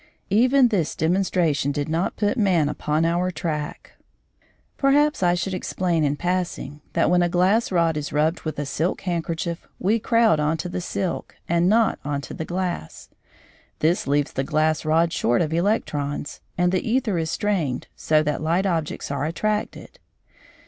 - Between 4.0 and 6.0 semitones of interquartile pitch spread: No, average, 3.6 semitones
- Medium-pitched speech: Yes, medium, 170 Hz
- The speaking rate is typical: Yes, average, 170 wpm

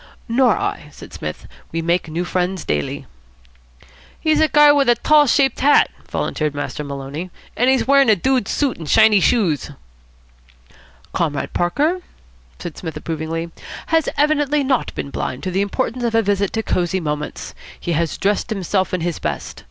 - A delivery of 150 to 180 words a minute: Yes, average, 165 wpm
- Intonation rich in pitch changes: Yes, wide, 8.2 semitones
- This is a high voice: Yes, high, 195 Hz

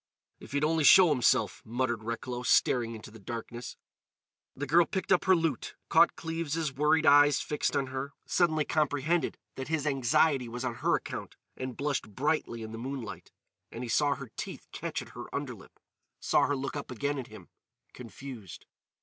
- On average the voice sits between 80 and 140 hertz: Yes, low, 135 Hz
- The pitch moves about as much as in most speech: Yes, average, 3.9 semitones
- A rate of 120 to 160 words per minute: No, average, 175 wpm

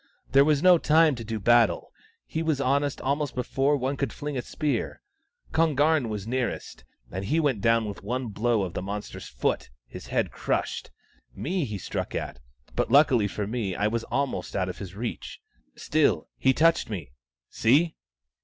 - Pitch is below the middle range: Yes, low, 125 Hz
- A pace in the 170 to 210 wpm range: Yes, average, 185 wpm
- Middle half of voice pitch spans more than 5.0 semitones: Yes, wide, 5.6 semitones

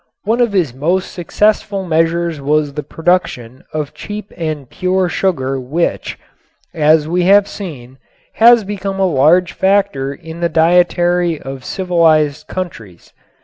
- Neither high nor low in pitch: Yes, medium, 170 Hz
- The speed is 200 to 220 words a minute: No, slow, 135 wpm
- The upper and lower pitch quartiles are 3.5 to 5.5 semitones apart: Yes, average, 4.1 semitones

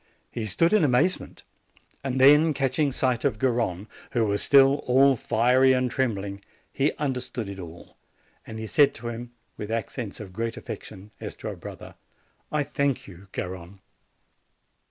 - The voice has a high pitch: No, low, 120 Hz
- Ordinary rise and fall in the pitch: Yes, average, 4.5 semitones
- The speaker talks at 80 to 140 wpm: No, average, 155 wpm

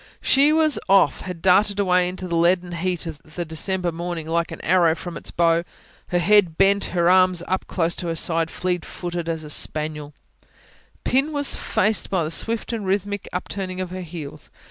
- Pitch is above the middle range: No, medium, 180 Hz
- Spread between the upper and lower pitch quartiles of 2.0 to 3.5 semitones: Yes, narrow, 2.6 semitones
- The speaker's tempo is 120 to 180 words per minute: No, average, 190 wpm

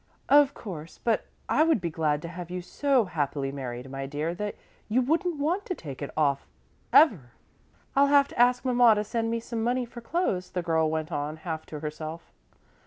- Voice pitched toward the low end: No, medium, 180 Hz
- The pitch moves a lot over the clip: Yes, wide, 8.3 semitones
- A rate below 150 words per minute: No, average, 200 wpm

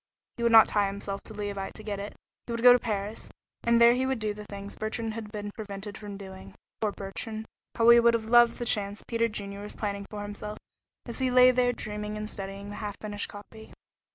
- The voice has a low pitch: No, high, 210 Hz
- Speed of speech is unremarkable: No, fast, 230 wpm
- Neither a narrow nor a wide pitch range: No, narrow, 2.3 semitones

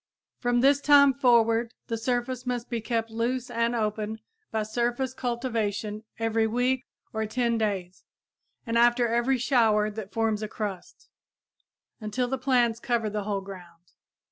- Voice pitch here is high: Yes, high, 230 Hz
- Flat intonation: Yes, narrow, 2.3 semitones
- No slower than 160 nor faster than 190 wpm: No, average, 145 wpm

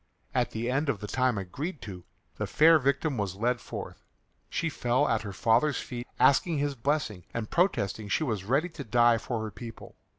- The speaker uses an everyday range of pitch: Yes, average, 4.8 semitones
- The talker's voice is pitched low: Yes, low, 120 Hz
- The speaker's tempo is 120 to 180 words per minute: No, average, 195 wpm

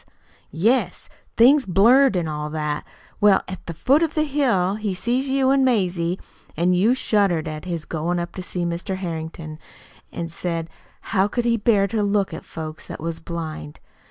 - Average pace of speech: Yes, average, 180 wpm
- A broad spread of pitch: Yes, wide, 5.7 semitones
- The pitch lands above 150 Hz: Yes, medium, 185 Hz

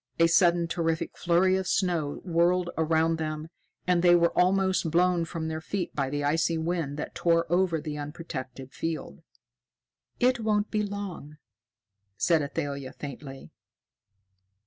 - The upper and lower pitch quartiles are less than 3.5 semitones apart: Yes, average, 2.8 semitones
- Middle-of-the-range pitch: Yes, medium, 165 Hz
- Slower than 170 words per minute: Yes, average, 140 wpm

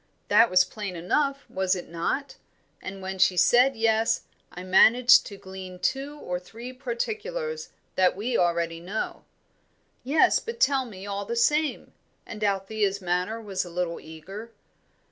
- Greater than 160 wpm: No, average, 150 wpm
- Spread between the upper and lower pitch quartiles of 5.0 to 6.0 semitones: Yes, wide, 5.4 semitones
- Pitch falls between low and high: No, high, 205 Hz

